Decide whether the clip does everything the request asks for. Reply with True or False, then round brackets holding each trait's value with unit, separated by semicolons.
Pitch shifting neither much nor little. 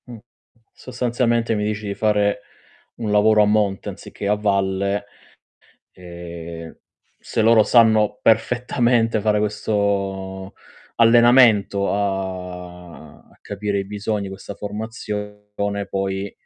False (2.0 semitones)